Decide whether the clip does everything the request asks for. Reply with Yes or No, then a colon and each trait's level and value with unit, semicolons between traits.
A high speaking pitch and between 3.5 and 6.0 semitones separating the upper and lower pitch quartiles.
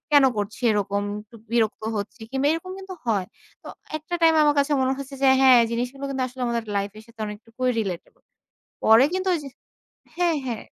Yes: very high, 250 Hz; average, 4.6 semitones